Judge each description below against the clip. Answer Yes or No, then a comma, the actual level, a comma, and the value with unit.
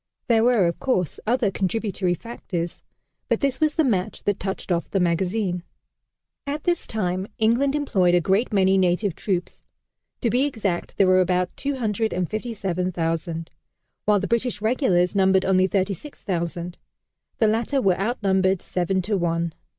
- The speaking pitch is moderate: No, high, 195 Hz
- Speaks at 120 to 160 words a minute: Yes, average, 145 wpm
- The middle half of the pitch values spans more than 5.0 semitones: No, average, 4.0 semitones